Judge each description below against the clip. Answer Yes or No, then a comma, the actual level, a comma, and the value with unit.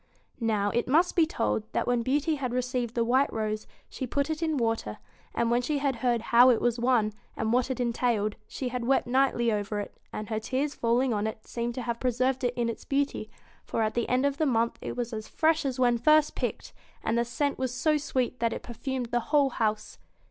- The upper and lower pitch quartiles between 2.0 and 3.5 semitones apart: Yes, narrow, 2.6 semitones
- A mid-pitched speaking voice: No, high, 245 Hz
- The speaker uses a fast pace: Yes, fast, 230 wpm